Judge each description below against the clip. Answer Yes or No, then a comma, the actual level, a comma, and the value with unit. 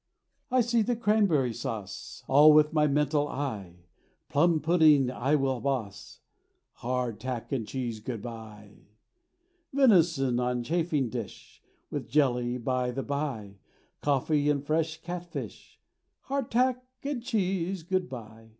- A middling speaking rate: No, slow, 130 wpm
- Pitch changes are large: Yes, wide, 5.8 semitones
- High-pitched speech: No, medium, 140 Hz